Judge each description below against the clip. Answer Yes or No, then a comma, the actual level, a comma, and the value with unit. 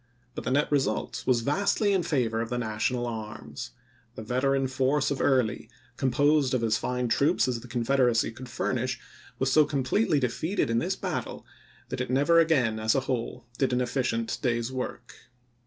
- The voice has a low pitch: Yes, low, 125 Hz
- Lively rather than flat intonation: No, average, 3.1 semitones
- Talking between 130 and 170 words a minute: No, average, 180 wpm